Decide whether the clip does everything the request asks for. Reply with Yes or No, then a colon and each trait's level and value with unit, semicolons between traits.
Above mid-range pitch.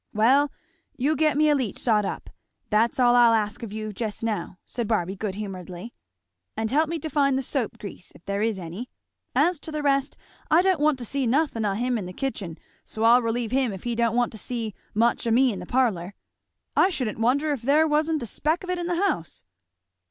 Yes: high, 240 Hz